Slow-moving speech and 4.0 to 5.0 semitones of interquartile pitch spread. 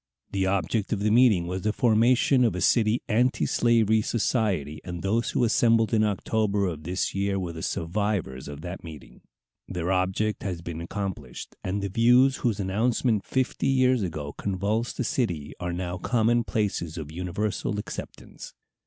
No: average, 160 wpm; average, 4.3 semitones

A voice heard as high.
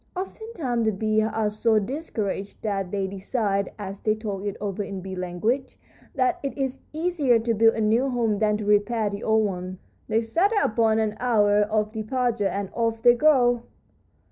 Yes: high, 220 Hz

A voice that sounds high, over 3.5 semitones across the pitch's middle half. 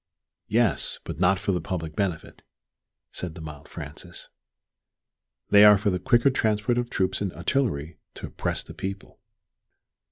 No: very low, 95 Hz; average, 4.1 semitones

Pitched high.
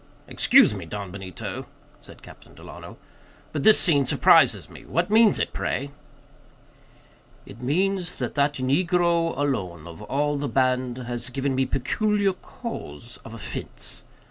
No: medium, 140 Hz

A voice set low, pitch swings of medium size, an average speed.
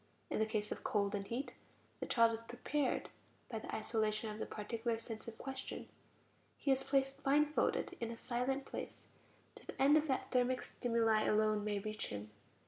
No: high, 230 Hz; average, 3.6 semitones; average, 180 wpm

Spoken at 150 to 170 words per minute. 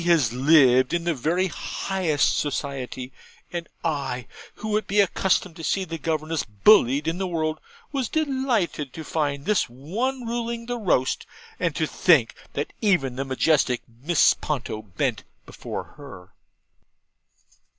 No: average, 140 wpm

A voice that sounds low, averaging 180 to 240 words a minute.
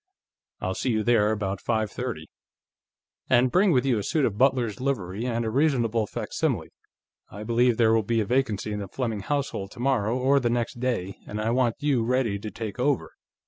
Yes: low, 115 Hz; average, 190 wpm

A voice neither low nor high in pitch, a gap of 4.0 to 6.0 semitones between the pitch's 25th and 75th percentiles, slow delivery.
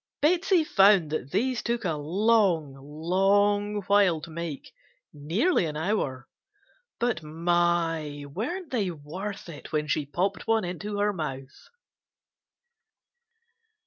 Yes: medium, 175 Hz; average, 5.3 semitones; slow, 115 wpm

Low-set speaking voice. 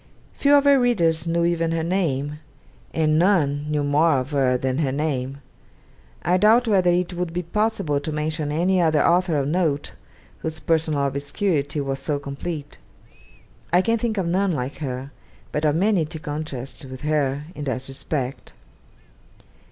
No: medium, 155 Hz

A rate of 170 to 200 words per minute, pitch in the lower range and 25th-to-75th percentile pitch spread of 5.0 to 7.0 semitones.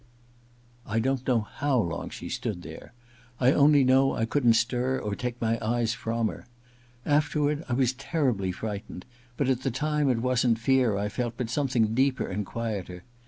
No: average, 180 wpm; low, 120 Hz; average, 3.1 semitones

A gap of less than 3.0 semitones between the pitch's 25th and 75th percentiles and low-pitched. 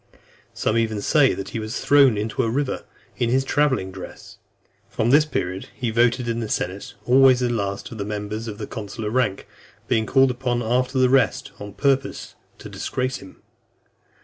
No: average, 3.5 semitones; low, 120 Hz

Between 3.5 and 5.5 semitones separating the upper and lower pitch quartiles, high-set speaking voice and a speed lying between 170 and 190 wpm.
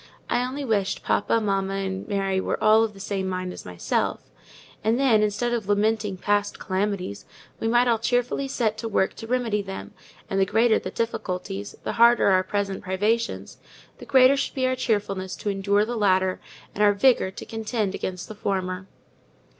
No: average, 3.1 semitones; high, 205 Hz; average, 185 wpm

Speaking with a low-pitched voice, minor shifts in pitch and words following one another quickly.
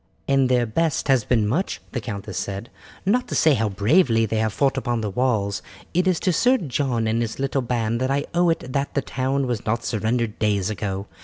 No: low, 125 Hz; average, 4.1 semitones; fast, 220 wpm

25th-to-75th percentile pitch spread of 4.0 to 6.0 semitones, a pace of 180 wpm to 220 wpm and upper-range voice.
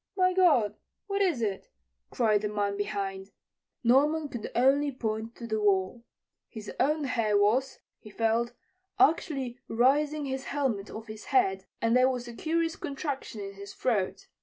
No: average, 5.1 semitones; average, 160 wpm; high, 240 Hz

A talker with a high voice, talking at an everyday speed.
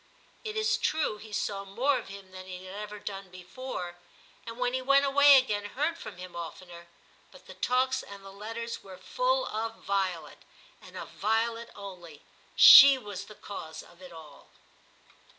Yes: high, 205 Hz; average, 175 wpm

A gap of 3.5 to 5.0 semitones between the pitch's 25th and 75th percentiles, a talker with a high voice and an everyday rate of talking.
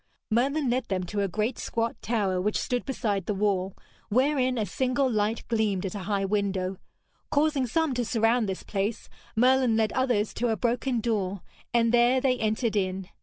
Yes: average, 3.8 semitones; high, 225 Hz; average, 180 wpm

